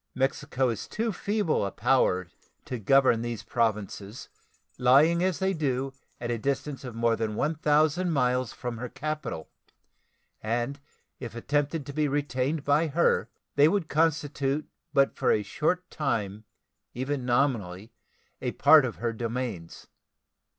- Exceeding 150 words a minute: No, average, 140 wpm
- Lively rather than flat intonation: No, average, 4.3 semitones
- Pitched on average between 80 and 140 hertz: Yes, low, 135 Hz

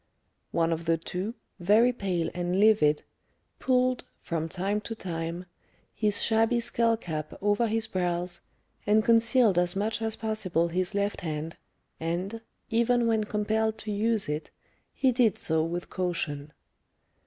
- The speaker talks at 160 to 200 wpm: No, average, 145 wpm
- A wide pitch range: No, average, 4.6 semitones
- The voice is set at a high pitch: Yes, high, 200 Hz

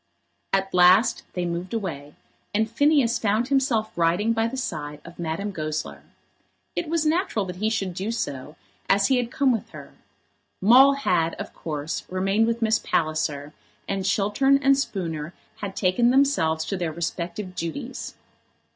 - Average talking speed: Yes, average, 155 wpm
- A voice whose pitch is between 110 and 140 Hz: No, high, 195 Hz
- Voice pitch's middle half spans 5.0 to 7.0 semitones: Yes, wide, 5.6 semitones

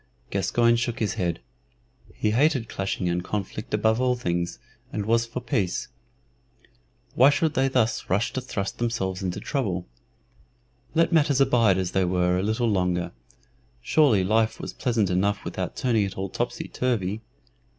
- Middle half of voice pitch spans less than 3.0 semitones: No, average, 4.7 semitones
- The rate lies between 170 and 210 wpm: No, average, 155 wpm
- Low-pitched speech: Yes, low, 110 Hz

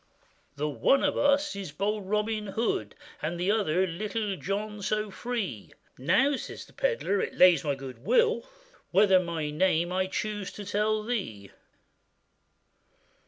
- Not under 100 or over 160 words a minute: Yes, average, 155 wpm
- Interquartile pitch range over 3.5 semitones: Yes, average, 4.3 semitones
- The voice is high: Yes, high, 200 Hz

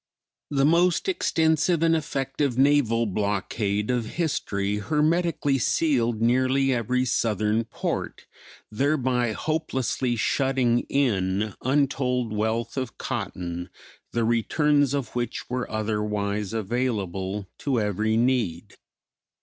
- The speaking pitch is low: Yes, low, 120 Hz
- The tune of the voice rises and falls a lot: No, average, 4.6 semitones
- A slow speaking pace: Yes, slow, 100 wpm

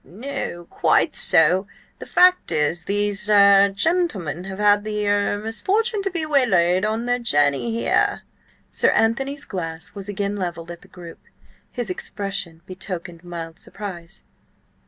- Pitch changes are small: No, average, 4.4 semitones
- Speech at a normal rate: No, slow, 120 wpm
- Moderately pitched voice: No, high, 200 Hz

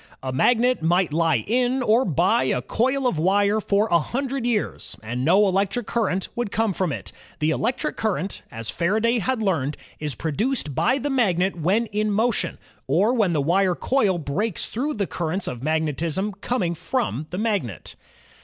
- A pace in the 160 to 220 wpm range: Yes, average, 175 wpm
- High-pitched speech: Yes, high, 195 Hz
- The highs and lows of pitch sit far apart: Yes, wide, 6.2 semitones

